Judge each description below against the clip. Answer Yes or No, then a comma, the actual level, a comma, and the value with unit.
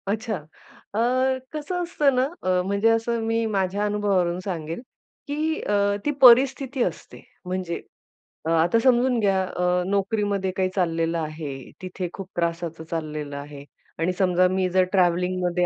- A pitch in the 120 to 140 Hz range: No, medium, 185 Hz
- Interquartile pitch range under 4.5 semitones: No, average, 4.8 semitones